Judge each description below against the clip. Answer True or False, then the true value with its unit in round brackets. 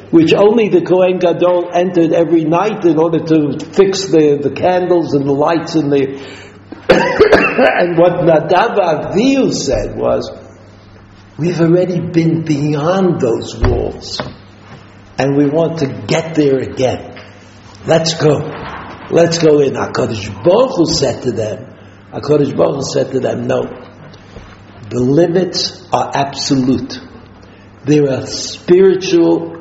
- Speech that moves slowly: True (125 wpm)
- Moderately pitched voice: True (150 Hz)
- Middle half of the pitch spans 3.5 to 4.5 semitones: False (5.6 semitones)